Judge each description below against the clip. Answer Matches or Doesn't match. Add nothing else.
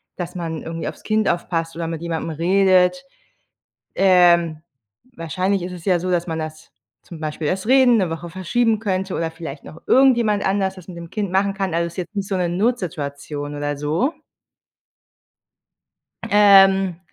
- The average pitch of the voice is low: Doesn't match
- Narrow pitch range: Doesn't match